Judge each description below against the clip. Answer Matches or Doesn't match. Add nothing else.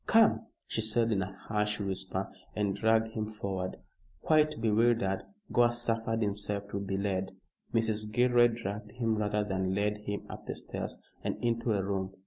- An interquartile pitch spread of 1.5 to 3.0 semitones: Matches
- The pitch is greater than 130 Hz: Doesn't match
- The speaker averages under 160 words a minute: Doesn't match